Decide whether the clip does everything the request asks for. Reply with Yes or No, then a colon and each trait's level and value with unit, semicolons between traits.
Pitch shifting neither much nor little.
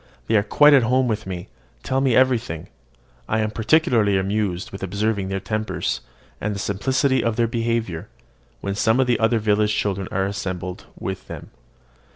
Yes: average, 3.2 semitones